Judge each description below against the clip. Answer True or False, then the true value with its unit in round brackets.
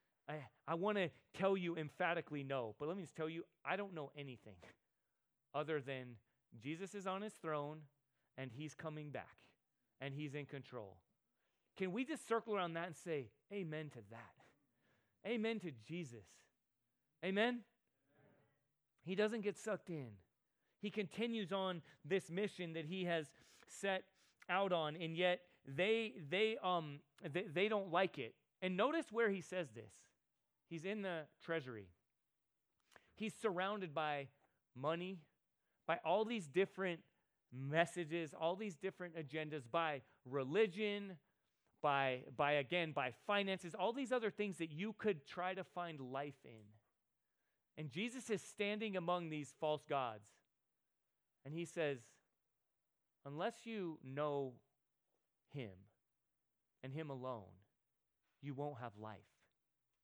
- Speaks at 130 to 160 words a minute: True (140 wpm)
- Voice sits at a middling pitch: True (165 Hz)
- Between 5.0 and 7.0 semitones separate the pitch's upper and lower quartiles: True (5.6 semitones)